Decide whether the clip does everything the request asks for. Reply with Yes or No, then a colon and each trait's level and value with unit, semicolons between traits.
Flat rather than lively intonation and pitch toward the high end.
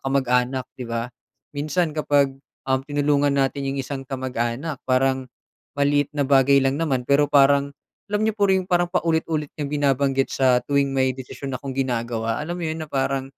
No: narrow, 1.8 semitones; medium, 140 Hz